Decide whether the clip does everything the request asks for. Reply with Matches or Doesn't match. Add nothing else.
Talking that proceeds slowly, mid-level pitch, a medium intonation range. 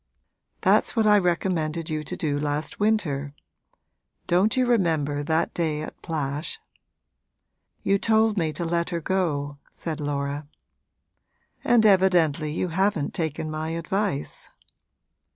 Matches